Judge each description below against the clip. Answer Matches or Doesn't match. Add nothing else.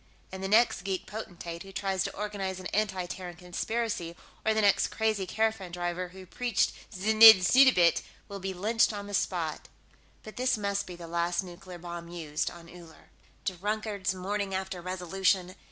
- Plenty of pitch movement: Doesn't match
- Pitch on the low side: Doesn't match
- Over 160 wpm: Matches